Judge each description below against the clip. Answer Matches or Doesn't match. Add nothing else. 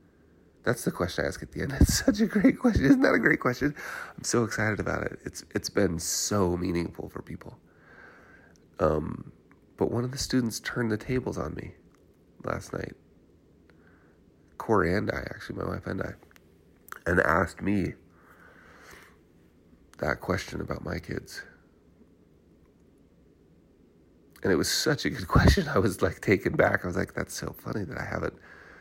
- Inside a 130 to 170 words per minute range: Matches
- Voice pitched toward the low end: Matches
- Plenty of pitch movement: Matches